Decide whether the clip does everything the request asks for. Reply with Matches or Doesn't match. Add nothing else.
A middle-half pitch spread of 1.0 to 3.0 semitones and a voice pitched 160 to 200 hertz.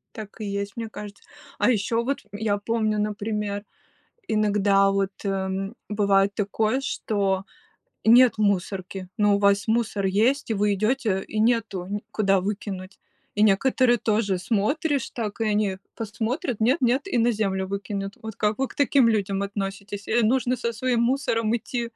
Doesn't match